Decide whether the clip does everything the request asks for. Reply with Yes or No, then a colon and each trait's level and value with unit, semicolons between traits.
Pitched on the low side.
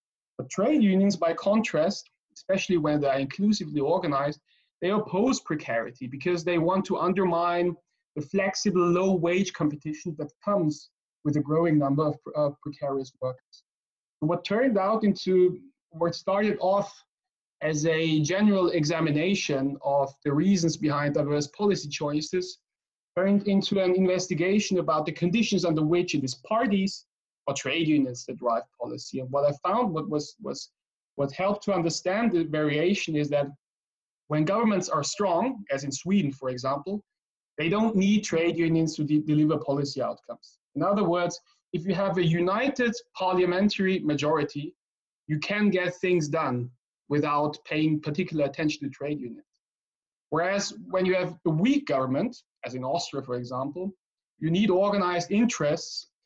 No: medium, 170 Hz